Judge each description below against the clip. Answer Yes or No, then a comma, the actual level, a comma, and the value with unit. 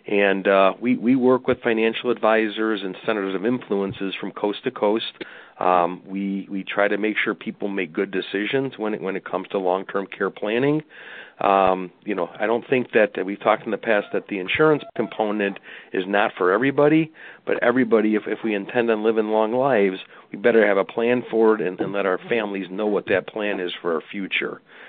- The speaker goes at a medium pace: No, fast, 210 wpm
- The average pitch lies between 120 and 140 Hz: No, low, 110 Hz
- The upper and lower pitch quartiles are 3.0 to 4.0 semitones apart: Yes, average, 3.3 semitones